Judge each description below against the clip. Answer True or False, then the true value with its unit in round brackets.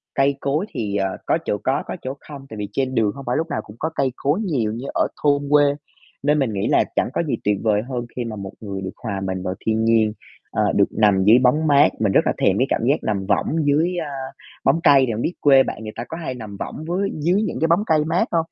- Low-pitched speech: True (130 Hz)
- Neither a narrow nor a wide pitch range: False (5.9 semitones)